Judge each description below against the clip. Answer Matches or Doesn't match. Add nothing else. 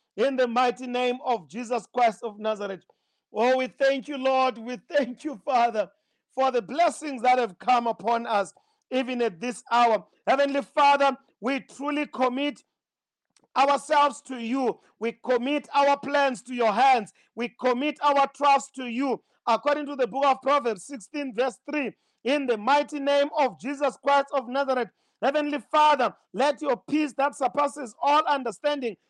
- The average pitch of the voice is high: Matches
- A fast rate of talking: Doesn't match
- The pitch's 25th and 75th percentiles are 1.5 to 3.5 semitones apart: Matches